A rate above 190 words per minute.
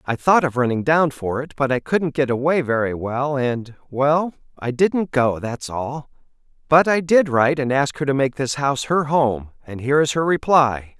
Yes: fast, 205 wpm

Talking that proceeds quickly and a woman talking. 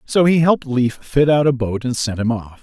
No: fast, 275 wpm; male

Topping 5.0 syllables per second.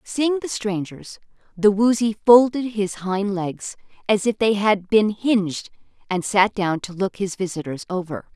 No: 4.2 syllables/s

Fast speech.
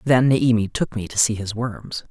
Yes: fast, 230 wpm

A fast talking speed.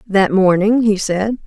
No: average, 165 wpm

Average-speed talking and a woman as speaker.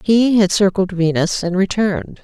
Yes: average, 160 wpm; female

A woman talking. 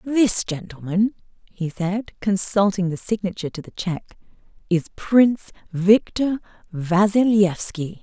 Yes: female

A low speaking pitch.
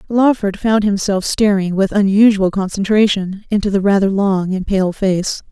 No: high, 200 Hz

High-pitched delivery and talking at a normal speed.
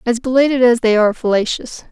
Yes: high, 235 Hz; average, 190 wpm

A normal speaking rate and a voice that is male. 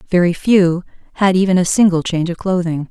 No: average, 185 wpm; female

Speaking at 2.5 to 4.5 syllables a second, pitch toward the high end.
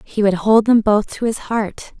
Yes: 4.4 syllables/s; high, 210 Hz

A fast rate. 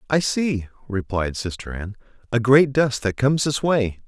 No: average, 175 wpm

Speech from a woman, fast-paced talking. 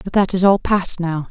Yes: female; fast, 275 wpm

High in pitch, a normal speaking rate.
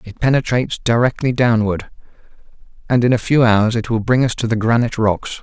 No: low, 115 Hz; average, 190 wpm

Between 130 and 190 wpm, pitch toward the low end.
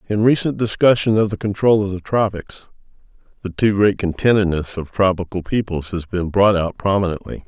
Yes: average, 170 wpm; low, 100 Hz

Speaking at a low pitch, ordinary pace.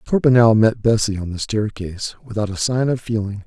Yes: low, 110 Hz; average, 190 wpm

